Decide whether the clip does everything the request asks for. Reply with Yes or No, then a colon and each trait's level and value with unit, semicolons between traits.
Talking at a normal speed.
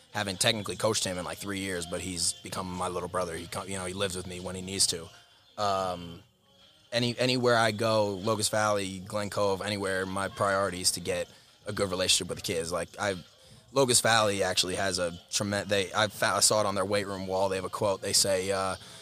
No: fast, 220 wpm